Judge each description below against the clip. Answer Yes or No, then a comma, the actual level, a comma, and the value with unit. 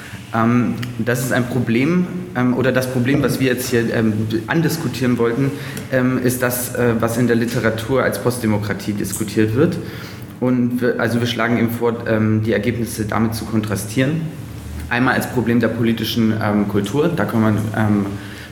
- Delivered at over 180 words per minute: No, average, 145 wpm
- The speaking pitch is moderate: No, low, 115 Hz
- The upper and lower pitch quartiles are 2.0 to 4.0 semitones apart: Yes, narrow, 2.4 semitones